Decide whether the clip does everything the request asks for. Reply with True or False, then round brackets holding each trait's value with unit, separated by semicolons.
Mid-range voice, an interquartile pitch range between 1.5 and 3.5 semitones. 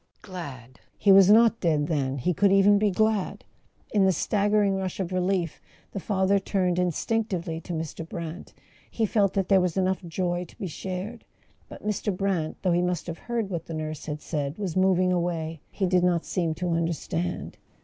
True (180 Hz; 2.9 semitones)